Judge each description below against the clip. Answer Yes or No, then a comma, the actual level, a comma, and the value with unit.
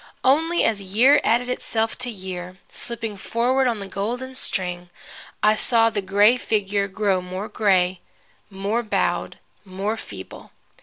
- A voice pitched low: No, high, 210 Hz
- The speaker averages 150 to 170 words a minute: No, average, 140 wpm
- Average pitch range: Yes, average, 3.7 semitones